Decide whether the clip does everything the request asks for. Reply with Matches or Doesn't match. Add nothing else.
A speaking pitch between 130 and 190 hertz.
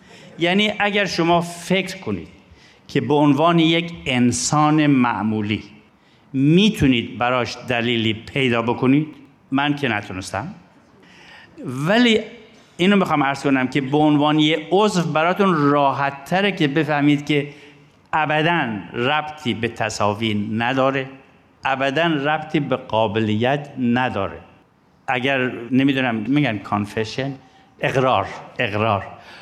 Matches